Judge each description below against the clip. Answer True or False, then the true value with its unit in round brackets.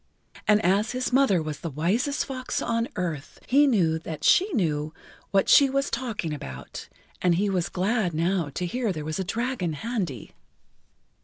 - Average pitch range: False (7.1 semitones)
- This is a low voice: False (190 Hz)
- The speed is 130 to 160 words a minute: False (175 wpm)